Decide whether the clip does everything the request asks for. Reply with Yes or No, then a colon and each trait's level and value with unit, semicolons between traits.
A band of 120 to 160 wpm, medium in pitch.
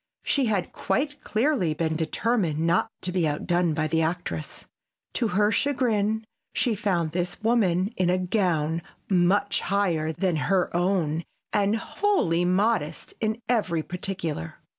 Yes: average, 140 wpm; medium, 180 Hz